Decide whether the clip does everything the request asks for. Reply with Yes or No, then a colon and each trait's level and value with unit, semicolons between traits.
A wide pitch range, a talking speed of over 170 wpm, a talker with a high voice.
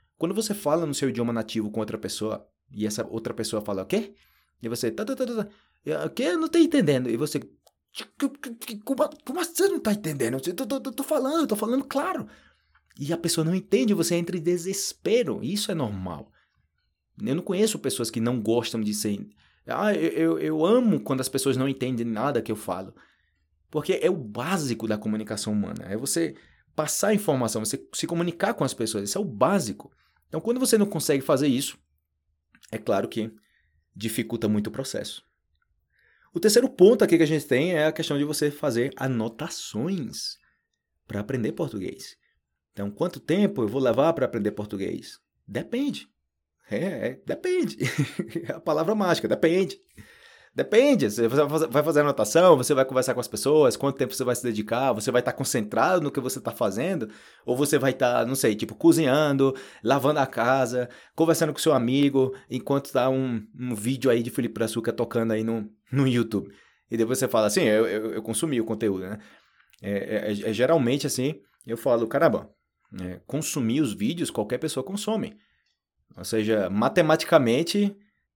No: wide, 7.9 semitones; average, 180 wpm; low, 135 Hz